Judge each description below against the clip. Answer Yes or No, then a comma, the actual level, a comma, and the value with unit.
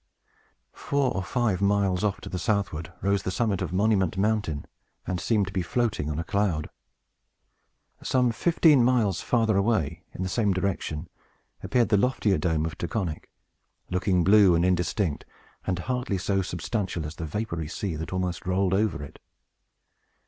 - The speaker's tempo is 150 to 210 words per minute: Yes, average, 160 wpm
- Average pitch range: Yes, average, 3.8 semitones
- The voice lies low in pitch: Yes, very low, 95 Hz